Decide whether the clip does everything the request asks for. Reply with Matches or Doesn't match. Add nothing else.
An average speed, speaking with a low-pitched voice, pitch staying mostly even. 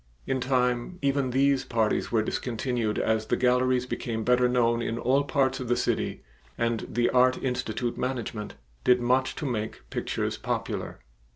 Matches